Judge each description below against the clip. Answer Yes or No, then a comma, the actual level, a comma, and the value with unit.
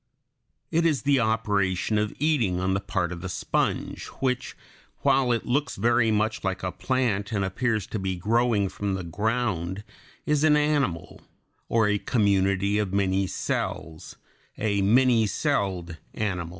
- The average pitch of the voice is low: Yes, low, 105 Hz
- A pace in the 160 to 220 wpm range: No, average, 150 wpm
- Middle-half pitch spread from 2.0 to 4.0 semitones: No, average, 4.4 semitones